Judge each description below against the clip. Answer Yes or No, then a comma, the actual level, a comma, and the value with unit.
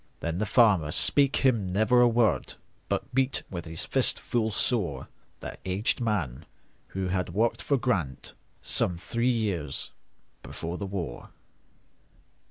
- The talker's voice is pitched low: Yes, low, 100 Hz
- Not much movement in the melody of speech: No, wide, 5.5 semitones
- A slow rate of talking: Yes, slow, 125 wpm